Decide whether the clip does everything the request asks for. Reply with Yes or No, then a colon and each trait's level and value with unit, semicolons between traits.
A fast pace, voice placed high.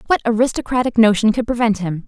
No: average, 175 wpm; high, 225 Hz